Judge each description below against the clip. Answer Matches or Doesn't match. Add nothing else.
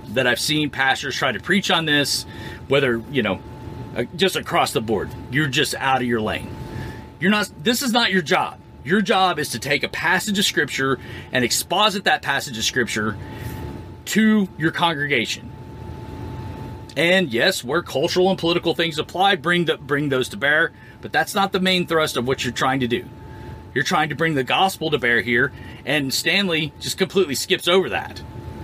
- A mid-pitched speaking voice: Matches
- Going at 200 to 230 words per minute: Doesn't match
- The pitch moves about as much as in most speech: Doesn't match